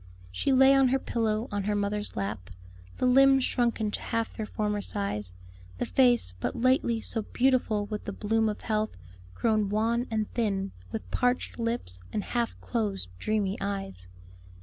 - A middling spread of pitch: Yes, average, 3.0 semitones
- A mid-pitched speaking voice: No, high, 215 Hz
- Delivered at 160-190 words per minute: Yes, average, 165 wpm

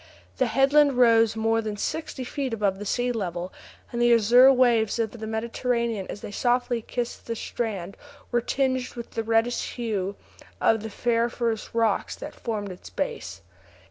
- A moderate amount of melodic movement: No, narrow, 2.1 semitones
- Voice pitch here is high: Yes, high, 230 Hz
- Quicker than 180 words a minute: No, average, 165 wpm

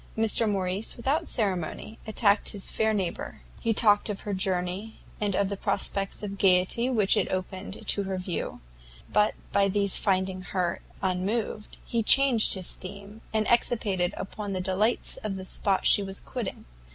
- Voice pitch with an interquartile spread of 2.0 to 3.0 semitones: Yes, narrow, 2.4 semitones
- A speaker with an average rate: Yes, average, 160 wpm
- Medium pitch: No, high, 200 Hz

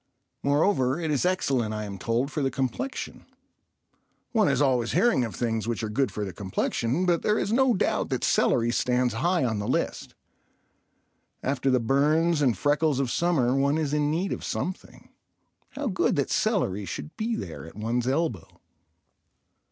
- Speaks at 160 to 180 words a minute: Yes, average, 175 wpm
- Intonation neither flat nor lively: No, wide, 6.3 semitones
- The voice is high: No, low, 135 Hz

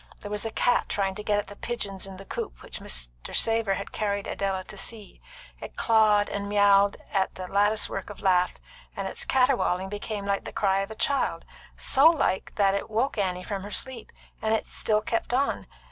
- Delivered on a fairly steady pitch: Yes, narrow, 2.3 semitones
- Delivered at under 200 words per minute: No, fast, 205 wpm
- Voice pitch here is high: Yes, high, 205 Hz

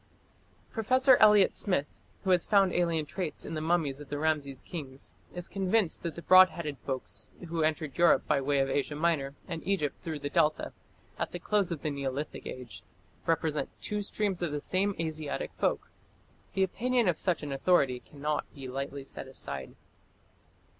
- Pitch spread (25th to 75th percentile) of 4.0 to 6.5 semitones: Yes, average, 4.6 semitones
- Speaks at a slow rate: No, average, 175 wpm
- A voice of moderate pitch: Yes, medium, 160 Hz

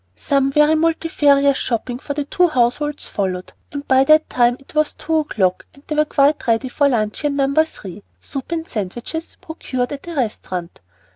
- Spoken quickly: No, average, 175 wpm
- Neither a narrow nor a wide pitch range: Yes, average, 4.1 semitones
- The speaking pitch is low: No, very high, 280 Hz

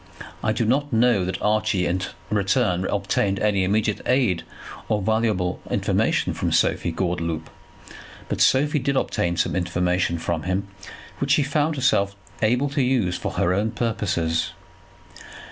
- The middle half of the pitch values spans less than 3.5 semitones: No, average, 5.2 semitones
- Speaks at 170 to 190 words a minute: No, average, 145 wpm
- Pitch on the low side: Yes, low, 100 Hz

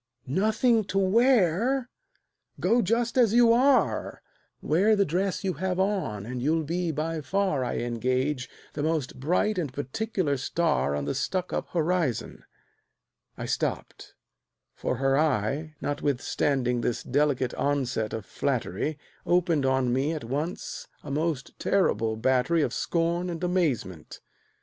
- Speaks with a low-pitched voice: No, medium, 155 Hz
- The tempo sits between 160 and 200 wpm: No, slow, 135 wpm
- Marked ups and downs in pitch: Yes, wide, 6.2 semitones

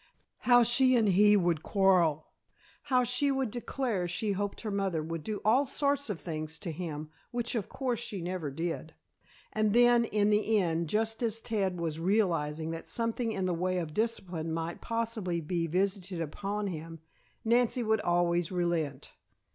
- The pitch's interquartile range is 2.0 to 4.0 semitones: No, average, 5.3 semitones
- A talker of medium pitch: No, high, 195 Hz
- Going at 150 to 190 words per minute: Yes, average, 170 wpm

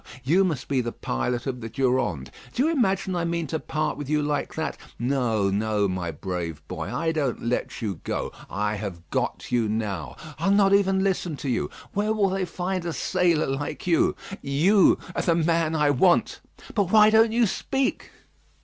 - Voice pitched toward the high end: No, medium, 150 Hz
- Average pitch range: No, wide, 8.9 semitones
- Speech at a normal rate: Yes, average, 190 wpm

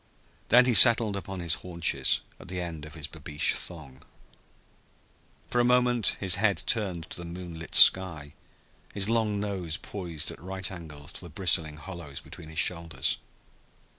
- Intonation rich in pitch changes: No, average, 4.0 semitones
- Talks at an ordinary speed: Yes, average, 160 wpm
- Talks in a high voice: No, very low, 90 Hz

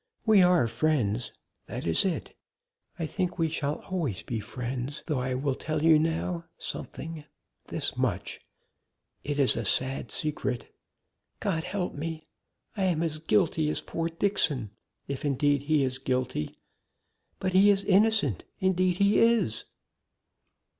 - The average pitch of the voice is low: No, medium, 155 Hz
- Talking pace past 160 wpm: No, average, 140 wpm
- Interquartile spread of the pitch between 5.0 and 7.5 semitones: Yes, wide, 5.6 semitones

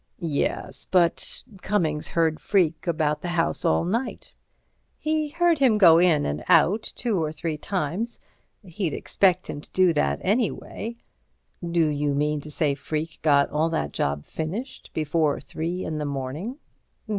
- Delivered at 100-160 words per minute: Yes, average, 155 wpm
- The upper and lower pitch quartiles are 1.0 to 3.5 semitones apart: No, average, 4.3 semitones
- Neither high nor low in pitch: Yes, medium, 165 Hz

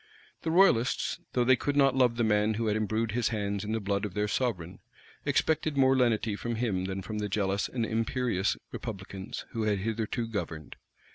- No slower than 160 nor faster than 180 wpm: No, average, 195 wpm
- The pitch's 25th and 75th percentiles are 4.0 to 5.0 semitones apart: No, average, 3.2 semitones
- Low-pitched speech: Yes, low, 110 Hz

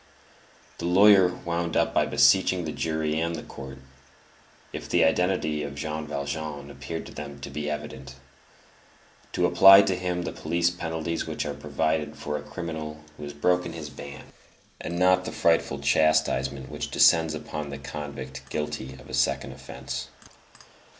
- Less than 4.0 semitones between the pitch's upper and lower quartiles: Yes, average, 2.9 semitones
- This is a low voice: Yes, very low, 75 Hz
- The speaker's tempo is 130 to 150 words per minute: No, average, 160 wpm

